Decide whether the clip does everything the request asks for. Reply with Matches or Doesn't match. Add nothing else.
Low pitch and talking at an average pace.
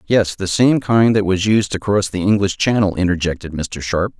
Doesn't match